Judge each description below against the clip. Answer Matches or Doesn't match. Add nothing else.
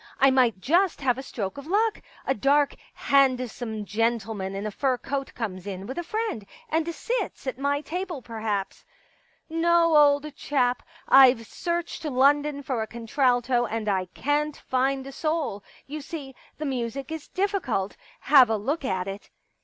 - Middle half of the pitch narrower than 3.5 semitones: Doesn't match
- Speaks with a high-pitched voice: Matches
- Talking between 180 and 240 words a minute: Doesn't match